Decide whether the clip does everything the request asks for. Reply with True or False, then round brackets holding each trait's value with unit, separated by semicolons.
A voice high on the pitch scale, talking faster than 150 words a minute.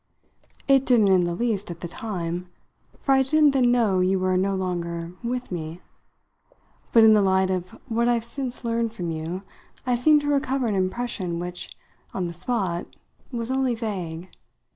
True (200 Hz; 175 wpm)